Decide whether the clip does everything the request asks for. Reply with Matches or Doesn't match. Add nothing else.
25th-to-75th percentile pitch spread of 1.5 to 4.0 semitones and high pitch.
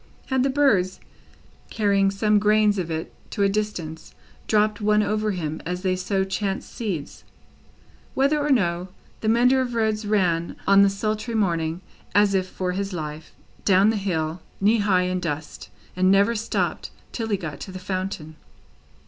Matches